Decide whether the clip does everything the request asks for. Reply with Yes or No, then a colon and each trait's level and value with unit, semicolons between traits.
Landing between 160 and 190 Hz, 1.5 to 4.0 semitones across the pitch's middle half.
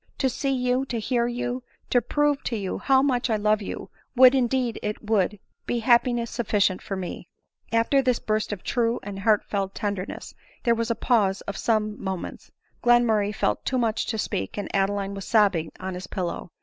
No: high, 220 Hz; average, 3.4 semitones